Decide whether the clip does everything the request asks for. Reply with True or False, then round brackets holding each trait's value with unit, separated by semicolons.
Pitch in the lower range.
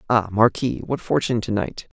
True (110 Hz)